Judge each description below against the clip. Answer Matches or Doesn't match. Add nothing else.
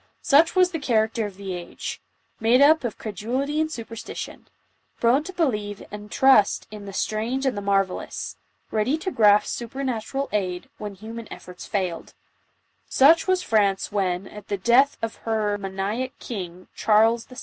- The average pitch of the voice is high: Matches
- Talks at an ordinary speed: Matches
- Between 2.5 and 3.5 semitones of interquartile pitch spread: Doesn't match